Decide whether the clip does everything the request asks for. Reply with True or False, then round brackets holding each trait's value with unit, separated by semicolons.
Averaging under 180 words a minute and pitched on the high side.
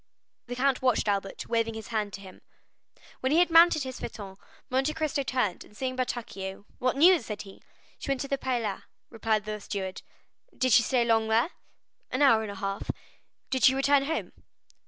False (190 wpm; 240 Hz)